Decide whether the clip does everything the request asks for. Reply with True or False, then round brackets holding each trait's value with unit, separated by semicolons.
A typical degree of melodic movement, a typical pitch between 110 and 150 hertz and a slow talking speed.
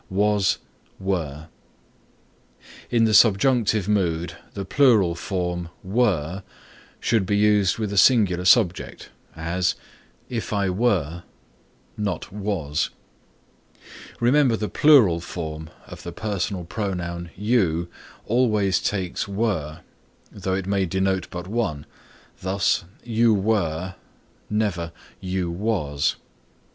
False (3.6 semitones; 95 Hz; 105 wpm)